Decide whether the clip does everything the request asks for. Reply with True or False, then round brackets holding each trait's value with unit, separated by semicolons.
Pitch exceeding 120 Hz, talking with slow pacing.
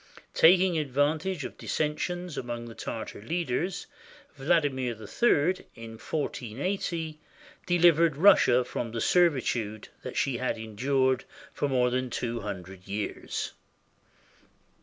True (135 Hz; 110 wpm)